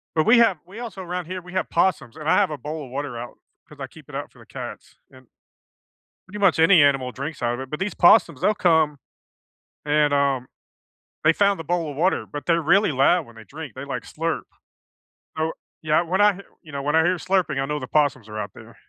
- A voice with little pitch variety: No, average, 4.2 semitones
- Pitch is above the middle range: No, medium, 155 Hz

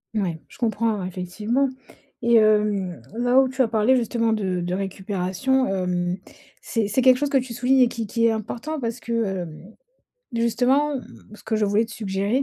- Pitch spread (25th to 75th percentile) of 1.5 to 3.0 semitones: No, average, 4.2 semitones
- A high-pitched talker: Yes, high, 225 Hz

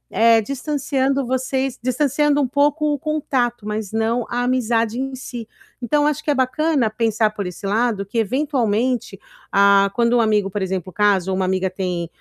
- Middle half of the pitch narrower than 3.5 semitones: No, average, 4.5 semitones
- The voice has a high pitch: Yes, high, 235 Hz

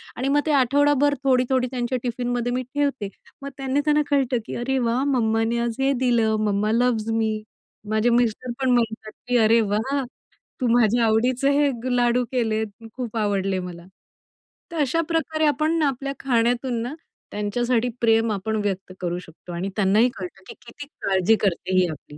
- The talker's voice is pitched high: Yes, high, 240 Hz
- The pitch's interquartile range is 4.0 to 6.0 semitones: No, average, 3.3 semitones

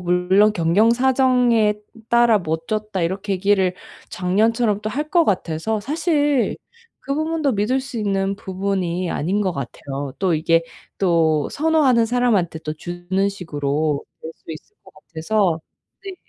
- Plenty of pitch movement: Yes, wide, 5.8 semitones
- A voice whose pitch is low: No, high, 195 Hz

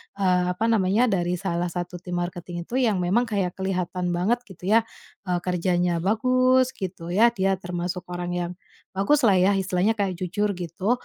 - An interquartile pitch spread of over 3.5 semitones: No, average, 2.9 semitones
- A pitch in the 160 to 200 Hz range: Yes, medium, 185 Hz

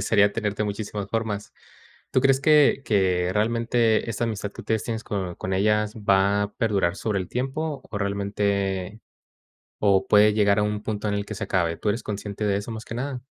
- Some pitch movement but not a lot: No, narrow, 2.1 semitones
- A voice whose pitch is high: No, low, 105 Hz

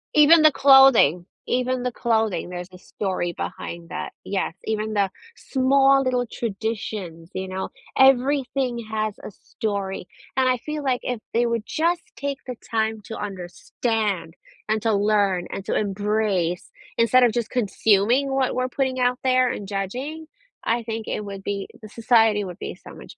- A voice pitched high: Yes, high, 220 Hz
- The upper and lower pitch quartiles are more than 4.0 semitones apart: Yes, average, 4.4 semitones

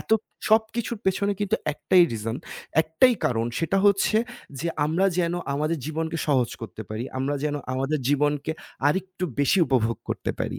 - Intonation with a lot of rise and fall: Yes, wide, 6.1 semitones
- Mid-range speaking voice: Yes, medium, 155 Hz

